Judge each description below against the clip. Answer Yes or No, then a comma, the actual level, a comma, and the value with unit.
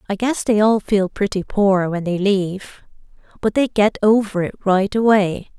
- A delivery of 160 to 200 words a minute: Yes, average, 185 wpm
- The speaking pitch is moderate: No, high, 200 Hz